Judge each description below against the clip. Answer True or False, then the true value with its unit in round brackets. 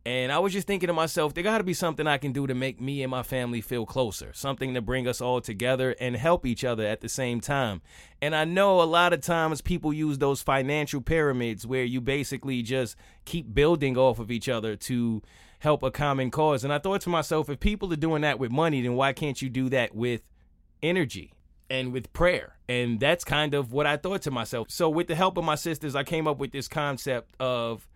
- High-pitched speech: False (135 Hz)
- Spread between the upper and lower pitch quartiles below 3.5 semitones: False (3.9 semitones)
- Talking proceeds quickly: True (235 wpm)